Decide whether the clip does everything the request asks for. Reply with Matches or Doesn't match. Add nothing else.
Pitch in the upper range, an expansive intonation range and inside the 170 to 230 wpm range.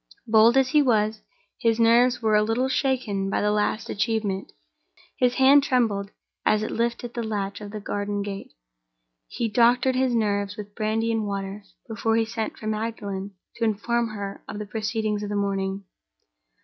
Doesn't match